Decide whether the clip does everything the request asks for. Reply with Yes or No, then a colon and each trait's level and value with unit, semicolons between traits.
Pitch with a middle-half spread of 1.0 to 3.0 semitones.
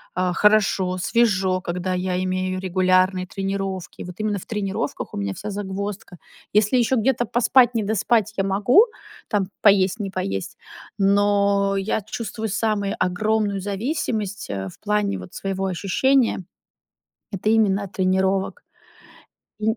Yes: narrow, 2.4 semitones